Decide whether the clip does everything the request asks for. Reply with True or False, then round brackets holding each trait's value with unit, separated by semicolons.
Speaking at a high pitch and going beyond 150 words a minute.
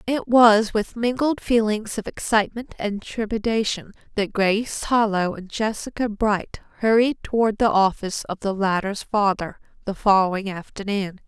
False (210 Hz; 140 wpm)